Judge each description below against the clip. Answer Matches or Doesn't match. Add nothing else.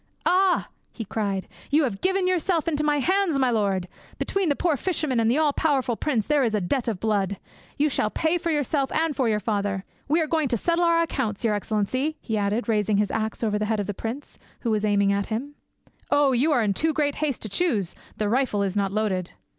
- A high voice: Matches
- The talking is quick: Matches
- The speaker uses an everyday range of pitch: Doesn't match